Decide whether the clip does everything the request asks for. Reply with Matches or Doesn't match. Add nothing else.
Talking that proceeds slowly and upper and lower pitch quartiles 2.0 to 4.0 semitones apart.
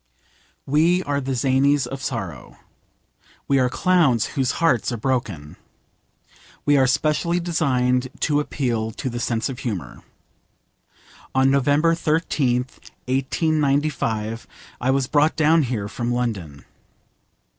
Matches